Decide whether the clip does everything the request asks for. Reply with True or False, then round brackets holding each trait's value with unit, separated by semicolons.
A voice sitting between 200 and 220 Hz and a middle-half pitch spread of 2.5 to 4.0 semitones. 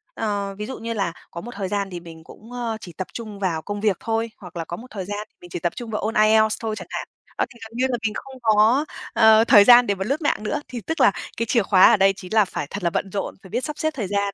True (210 Hz; 3.0 semitones)